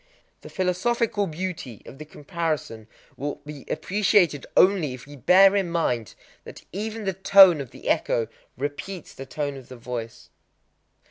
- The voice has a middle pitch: Yes, medium, 160 Hz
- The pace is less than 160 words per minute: Yes, average, 150 wpm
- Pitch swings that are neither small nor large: No, wide, 6.1 semitones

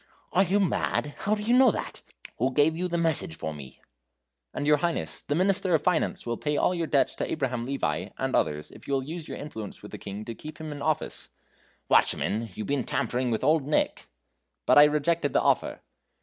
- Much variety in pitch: No, average, 4.9 semitones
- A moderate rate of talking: No, fast, 215 wpm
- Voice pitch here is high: No, medium, 150 Hz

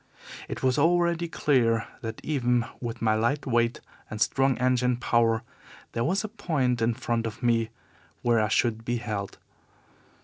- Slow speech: No, average, 160 wpm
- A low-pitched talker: Yes, low, 120 Hz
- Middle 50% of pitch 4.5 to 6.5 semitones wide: No, average, 2.7 semitones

